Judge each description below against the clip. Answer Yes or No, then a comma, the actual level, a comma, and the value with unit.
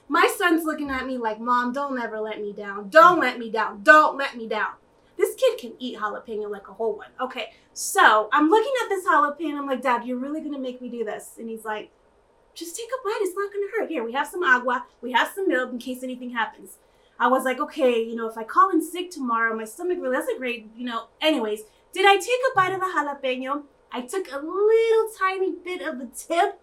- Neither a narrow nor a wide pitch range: No, wide, 7.9 semitones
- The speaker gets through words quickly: Yes, fast, 240 wpm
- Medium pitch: No, very high, 290 Hz